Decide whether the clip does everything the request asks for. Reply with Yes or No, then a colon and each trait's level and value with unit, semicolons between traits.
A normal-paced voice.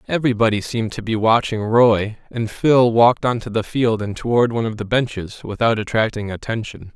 Yes: average, 190 wpm